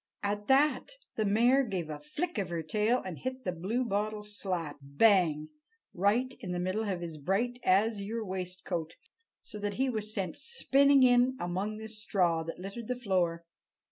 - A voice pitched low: No, high, 205 Hz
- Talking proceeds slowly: No, average, 170 wpm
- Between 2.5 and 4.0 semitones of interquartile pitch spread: No, average, 4.9 semitones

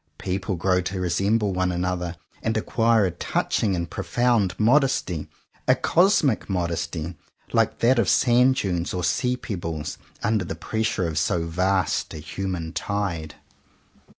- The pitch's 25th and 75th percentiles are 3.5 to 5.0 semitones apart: Yes, average, 4.4 semitones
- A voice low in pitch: Yes, very low, 95 Hz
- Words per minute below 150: Yes, average, 140 wpm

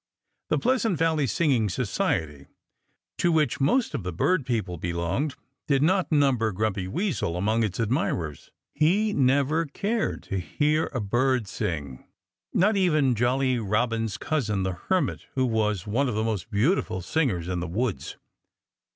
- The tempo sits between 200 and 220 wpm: No, average, 150 wpm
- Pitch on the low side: Yes, low, 120 Hz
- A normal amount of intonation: No, wide, 7.6 semitones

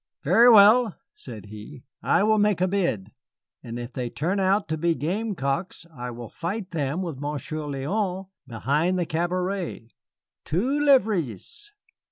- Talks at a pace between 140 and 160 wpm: Yes, average, 145 wpm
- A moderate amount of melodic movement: No, wide, 6.7 semitones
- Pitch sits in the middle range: Yes, medium, 170 Hz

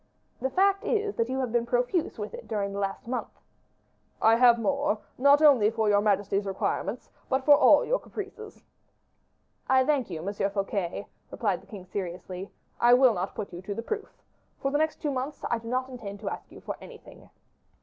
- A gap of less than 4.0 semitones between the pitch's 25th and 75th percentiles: No, wide, 5.6 semitones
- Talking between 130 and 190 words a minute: No, average, 200 wpm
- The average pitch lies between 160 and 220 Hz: No, high, 235 Hz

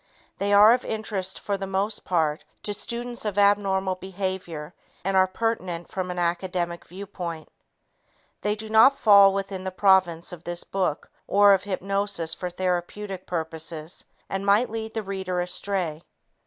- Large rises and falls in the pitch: No, narrow, 2.4 semitones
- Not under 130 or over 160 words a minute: Yes, average, 155 wpm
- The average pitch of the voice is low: No, high, 190 Hz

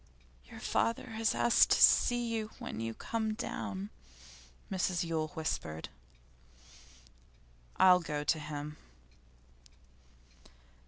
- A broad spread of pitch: Yes, wide, 7.0 semitones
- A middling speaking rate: No, slow, 100 wpm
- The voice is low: No, medium, 165 Hz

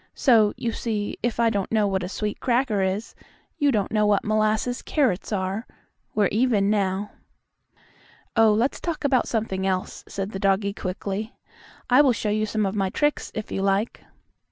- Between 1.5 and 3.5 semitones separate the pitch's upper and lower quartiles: Yes, average, 2.8 semitones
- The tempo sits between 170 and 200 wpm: Yes, average, 180 wpm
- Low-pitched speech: No, high, 210 Hz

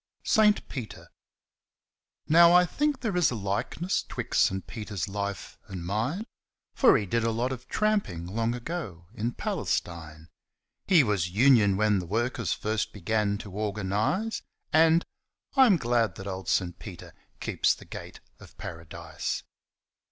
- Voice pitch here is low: Yes, low, 110 Hz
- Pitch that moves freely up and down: Yes, wide, 8.6 semitones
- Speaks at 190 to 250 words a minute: No, average, 145 wpm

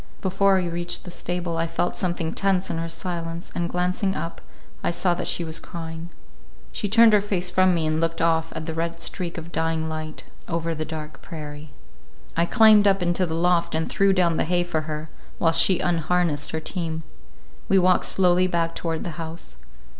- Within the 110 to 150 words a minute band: No, average, 200 wpm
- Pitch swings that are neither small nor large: No, narrow, 1.8 semitones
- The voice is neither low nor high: Yes, medium, 170 Hz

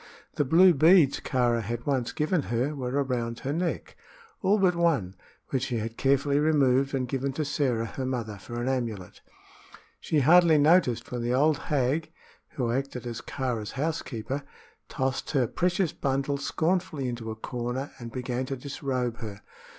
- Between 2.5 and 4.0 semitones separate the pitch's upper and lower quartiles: Yes, average, 3.5 semitones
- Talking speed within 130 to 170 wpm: Yes, average, 165 wpm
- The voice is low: Yes, low, 130 Hz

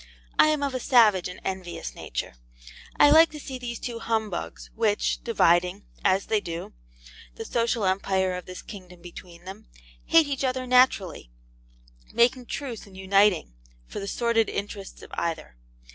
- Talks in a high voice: Yes, high, 205 Hz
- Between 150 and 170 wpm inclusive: Yes, average, 160 wpm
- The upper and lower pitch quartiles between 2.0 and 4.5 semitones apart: No, average, 4.9 semitones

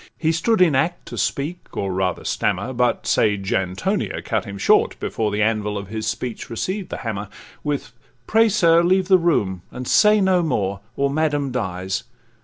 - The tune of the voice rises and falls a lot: Yes, wide, 9.0 semitones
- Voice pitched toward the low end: Yes, low, 125 Hz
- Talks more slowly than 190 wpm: Yes, average, 180 wpm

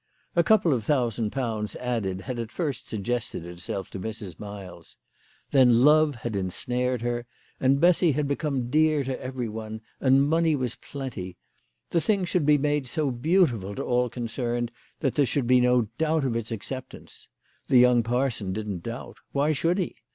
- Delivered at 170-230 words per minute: Yes, average, 175 wpm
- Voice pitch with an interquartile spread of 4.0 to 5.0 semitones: Yes, average, 4.5 semitones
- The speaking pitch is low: Yes, low, 125 Hz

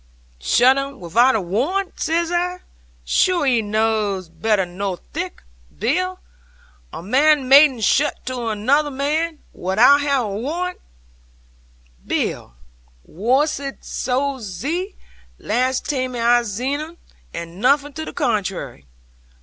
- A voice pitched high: Yes, very high, 255 Hz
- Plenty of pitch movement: Yes, wide, 5.7 semitones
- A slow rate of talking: Yes, slow, 120 wpm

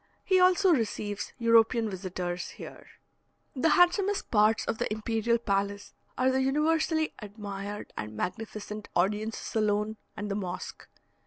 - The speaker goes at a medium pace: No, slow, 130 wpm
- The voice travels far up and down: No, average, 4.4 semitones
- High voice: Yes, high, 215 Hz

